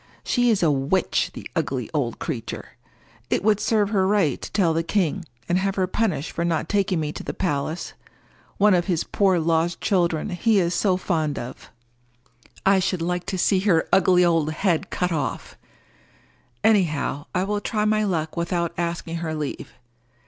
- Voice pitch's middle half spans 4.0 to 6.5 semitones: No, average, 3.3 semitones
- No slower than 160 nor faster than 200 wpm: Yes, average, 175 wpm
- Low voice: No, medium, 175 Hz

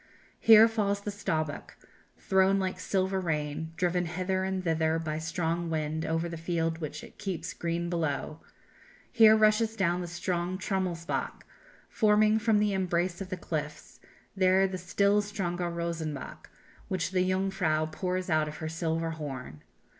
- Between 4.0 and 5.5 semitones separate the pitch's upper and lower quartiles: No, average, 2.9 semitones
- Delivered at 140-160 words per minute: Yes, average, 150 wpm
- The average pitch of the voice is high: No, medium, 175 Hz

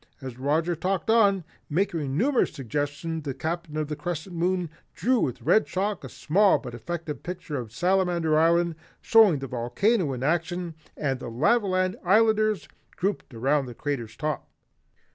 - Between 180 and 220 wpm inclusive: No, average, 155 wpm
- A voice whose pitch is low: No, medium, 165 Hz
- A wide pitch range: No, average, 4.6 semitones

